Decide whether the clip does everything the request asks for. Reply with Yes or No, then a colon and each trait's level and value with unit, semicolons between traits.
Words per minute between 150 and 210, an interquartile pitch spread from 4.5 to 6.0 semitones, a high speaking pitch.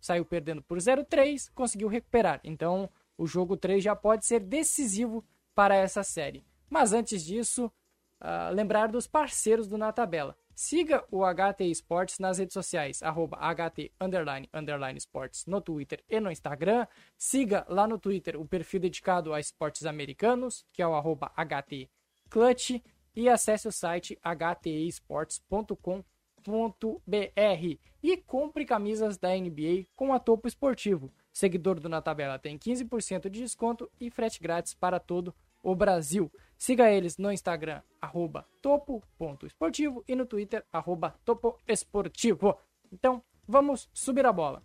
No: average, 140 wpm; wide, 5.5 semitones; high, 195 Hz